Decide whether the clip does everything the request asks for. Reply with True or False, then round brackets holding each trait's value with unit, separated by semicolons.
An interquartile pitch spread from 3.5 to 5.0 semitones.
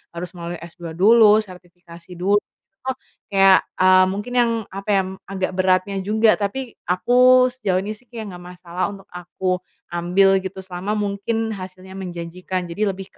False (2.5 semitones)